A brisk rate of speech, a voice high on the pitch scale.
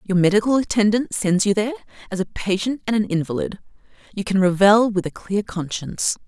No: average, 180 wpm; high, 205 Hz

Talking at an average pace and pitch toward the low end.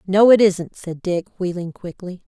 No: average, 180 wpm; medium, 185 Hz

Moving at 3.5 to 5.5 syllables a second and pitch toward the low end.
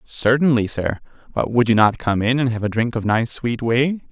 Yes: 5.0 syllables/s; low, 120 Hz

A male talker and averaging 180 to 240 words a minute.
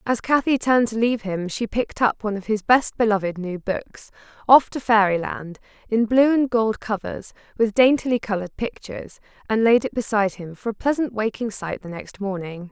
No: female; average, 185 wpm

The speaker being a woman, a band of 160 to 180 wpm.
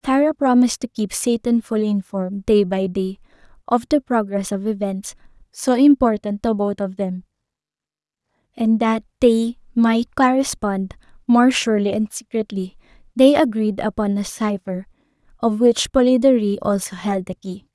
No: female; average, 140 wpm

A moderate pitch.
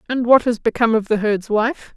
No: high, 230 Hz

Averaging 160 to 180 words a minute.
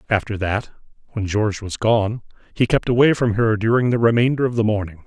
No: average, 200 wpm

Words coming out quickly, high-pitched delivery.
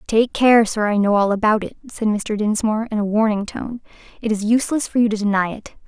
Yes: fast, 235 wpm; high, 215 Hz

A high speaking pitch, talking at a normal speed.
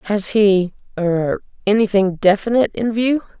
No: high, 205 Hz; slow, 90 wpm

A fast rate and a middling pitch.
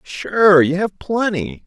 No: slow, 110 wpm; medium, 175 Hz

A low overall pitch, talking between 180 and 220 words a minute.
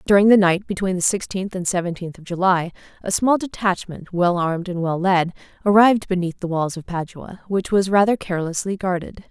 No: medium, 185 Hz; average, 185 wpm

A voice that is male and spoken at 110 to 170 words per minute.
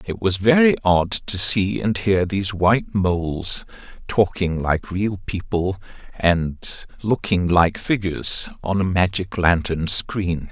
Yes: male; slow, 135 wpm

